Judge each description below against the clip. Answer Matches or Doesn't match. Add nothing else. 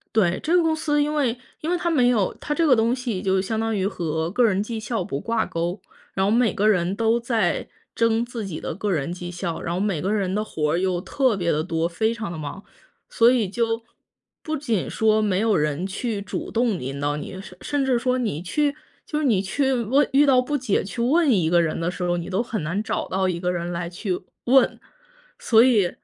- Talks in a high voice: Matches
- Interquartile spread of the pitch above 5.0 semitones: Matches